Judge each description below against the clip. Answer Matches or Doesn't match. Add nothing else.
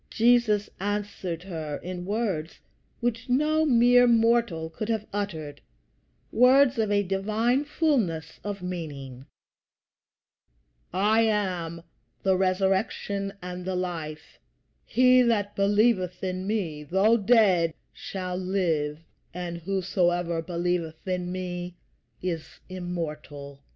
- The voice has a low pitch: Doesn't match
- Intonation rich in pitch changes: Doesn't match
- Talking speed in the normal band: Doesn't match